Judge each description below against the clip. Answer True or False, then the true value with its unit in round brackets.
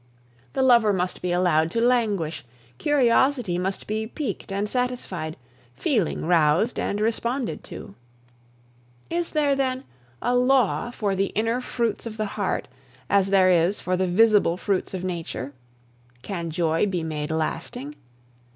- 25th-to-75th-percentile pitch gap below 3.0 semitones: False (5.4 semitones)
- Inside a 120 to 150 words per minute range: True (140 wpm)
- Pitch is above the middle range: True (200 Hz)